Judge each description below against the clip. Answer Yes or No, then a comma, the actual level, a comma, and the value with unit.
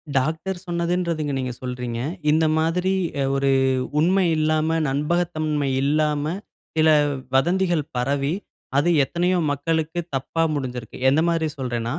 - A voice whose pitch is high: No, medium, 155 Hz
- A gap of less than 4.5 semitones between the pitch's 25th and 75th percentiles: Yes, average, 3.7 semitones